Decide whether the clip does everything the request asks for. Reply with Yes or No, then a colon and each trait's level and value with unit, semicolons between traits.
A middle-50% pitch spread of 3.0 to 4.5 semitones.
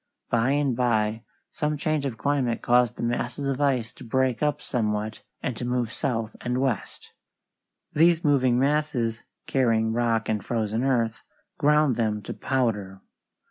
Yes: average, 3.5 semitones